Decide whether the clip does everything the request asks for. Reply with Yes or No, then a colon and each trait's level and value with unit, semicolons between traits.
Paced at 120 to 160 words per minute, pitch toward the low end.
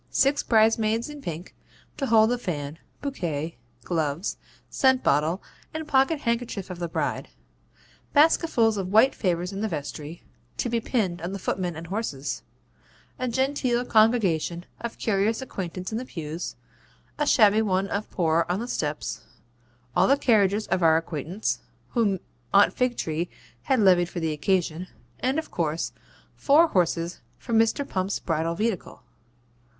No: average, 155 wpm; high, 195 Hz